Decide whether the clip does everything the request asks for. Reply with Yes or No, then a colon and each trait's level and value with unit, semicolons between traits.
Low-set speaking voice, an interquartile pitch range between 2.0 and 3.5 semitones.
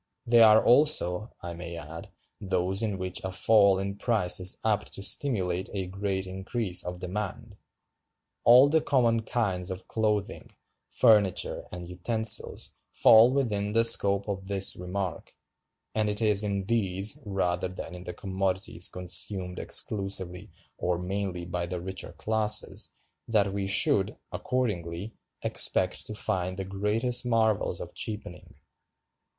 Yes: low, 100 Hz; average, 3.2 semitones